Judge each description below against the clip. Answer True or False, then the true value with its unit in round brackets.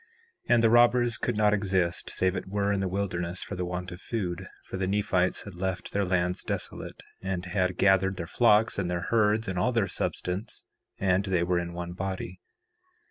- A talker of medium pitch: False (95 Hz)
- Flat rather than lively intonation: True (2.3 semitones)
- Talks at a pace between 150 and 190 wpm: False (200 wpm)